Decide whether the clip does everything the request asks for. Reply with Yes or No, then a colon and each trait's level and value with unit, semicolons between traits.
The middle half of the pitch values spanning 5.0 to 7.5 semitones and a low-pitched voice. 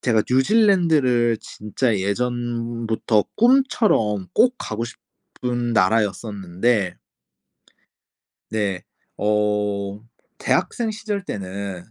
No: average, 3.9 semitones; low, 115 Hz